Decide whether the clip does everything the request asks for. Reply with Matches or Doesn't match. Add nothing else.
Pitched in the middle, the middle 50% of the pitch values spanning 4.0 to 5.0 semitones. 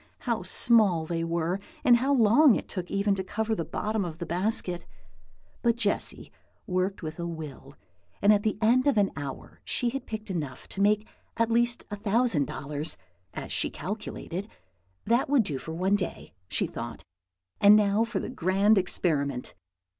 Doesn't match